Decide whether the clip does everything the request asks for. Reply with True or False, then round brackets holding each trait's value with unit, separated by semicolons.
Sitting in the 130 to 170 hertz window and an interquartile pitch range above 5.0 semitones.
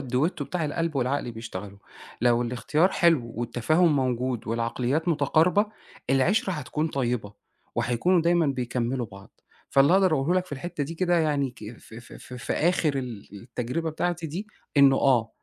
True (135 Hz; 5.5 semitones)